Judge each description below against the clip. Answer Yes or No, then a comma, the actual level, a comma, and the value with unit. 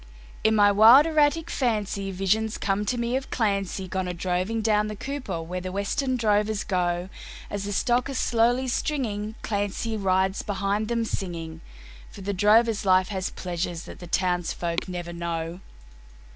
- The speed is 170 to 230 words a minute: No, average, 160 wpm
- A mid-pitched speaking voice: No, high, 205 Hz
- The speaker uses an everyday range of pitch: Yes, average, 3.7 semitones